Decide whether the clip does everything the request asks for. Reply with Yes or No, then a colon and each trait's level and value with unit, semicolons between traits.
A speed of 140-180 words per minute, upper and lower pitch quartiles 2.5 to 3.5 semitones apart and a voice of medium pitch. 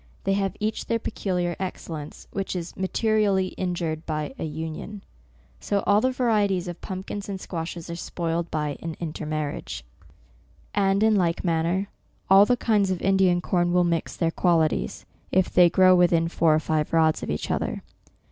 Yes: average, 175 wpm; average, 3.0 semitones; medium, 180 Hz